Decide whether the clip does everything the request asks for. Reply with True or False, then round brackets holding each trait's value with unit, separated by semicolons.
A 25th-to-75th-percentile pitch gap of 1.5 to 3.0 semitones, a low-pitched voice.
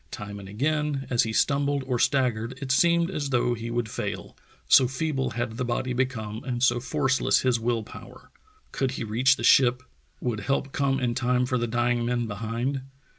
True (2.4 semitones; 125 Hz)